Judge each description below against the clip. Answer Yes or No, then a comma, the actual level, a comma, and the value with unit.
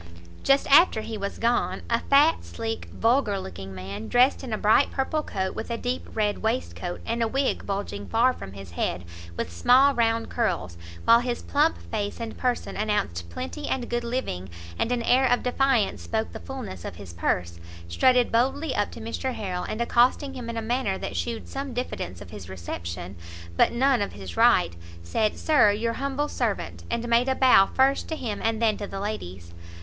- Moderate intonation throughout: No, wide, 6.0 semitones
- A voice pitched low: No, high, 230 Hz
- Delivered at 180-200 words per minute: Yes, average, 195 wpm